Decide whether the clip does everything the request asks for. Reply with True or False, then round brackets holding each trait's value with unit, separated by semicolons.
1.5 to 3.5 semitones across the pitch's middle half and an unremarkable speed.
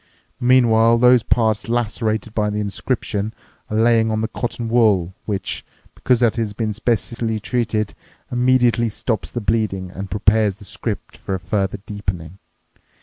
True (2.4 semitones; 145 wpm)